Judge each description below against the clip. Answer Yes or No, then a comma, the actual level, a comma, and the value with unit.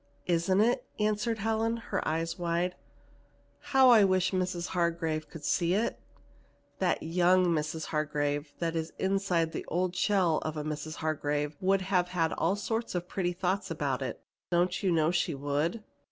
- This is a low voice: No, medium, 175 Hz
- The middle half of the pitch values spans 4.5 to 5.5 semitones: No, average, 3.2 semitones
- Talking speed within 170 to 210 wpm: No, average, 160 wpm